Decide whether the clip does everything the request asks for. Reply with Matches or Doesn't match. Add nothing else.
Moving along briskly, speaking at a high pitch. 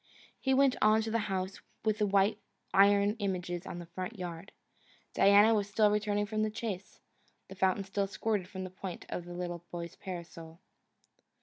Doesn't match